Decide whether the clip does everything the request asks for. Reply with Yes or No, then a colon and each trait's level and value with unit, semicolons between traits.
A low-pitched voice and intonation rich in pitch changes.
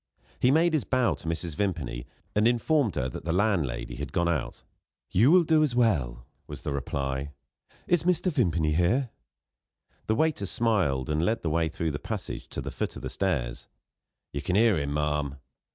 Yes: very low, 85 Hz; wide, 8.7 semitones